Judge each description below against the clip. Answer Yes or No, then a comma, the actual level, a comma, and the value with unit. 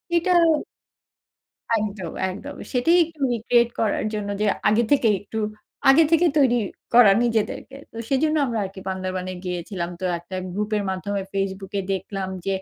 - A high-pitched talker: Yes, high, 210 Hz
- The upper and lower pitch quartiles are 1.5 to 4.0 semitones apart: No, average, 4.4 semitones